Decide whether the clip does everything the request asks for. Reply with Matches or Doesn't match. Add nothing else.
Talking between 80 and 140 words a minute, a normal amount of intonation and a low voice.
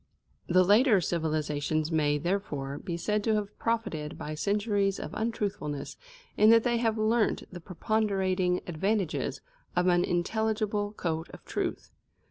Doesn't match